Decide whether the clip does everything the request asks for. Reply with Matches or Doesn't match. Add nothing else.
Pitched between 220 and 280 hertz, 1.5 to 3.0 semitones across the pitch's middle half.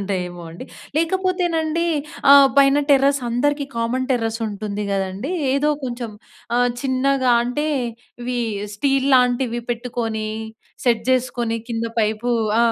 Doesn't match